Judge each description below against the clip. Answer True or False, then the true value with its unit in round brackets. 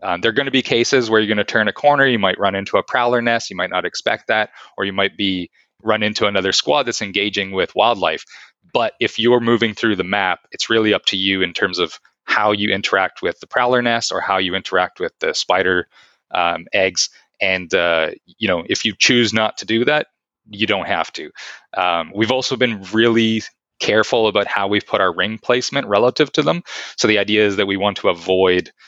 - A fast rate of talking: True (225 wpm)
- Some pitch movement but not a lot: True (3.2 semitones)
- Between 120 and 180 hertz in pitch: False (110 Hz)